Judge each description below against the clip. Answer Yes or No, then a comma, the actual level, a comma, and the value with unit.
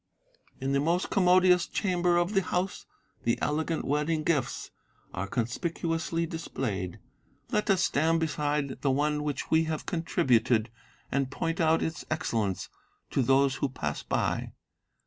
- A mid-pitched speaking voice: Yes, medium, 155 Hz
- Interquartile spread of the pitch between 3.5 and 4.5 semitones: Yes, average, 3.9 semitones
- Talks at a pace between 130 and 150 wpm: Yes, average, 140 wpm